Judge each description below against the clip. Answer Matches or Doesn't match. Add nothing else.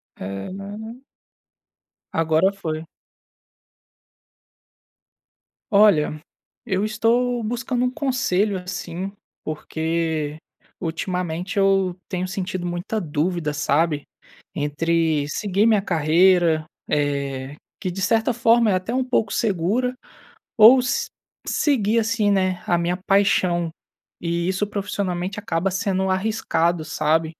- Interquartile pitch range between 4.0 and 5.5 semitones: Matches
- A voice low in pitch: Doesn't match